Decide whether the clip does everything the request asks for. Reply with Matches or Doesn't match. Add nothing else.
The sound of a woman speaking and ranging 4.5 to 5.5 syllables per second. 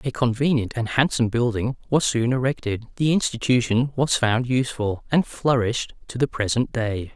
Doesn't match